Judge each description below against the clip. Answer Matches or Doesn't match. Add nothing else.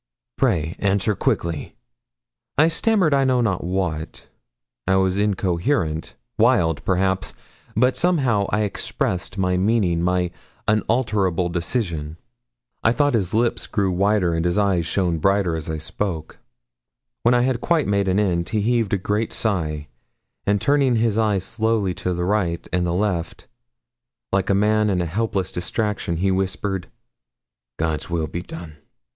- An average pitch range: Matches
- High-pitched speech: Doesn't match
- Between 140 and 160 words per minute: Matches